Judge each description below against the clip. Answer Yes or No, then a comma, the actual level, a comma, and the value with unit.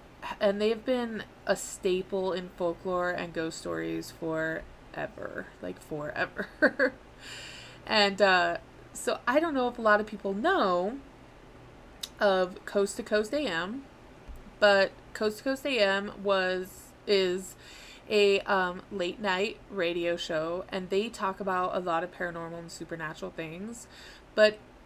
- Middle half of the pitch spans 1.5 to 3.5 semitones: Yes, average, 3.0 semitones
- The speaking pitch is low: No, high, 190 Hz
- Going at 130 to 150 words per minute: Yes, slow, 135 wpm